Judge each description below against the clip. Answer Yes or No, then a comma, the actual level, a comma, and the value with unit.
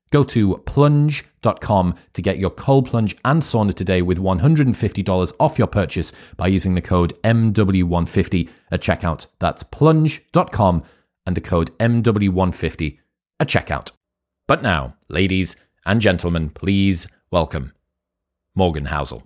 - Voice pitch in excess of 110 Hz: No, very low, 95 Hz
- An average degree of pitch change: Yes, average, 4.3 semitones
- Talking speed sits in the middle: No, slow, 125 wpm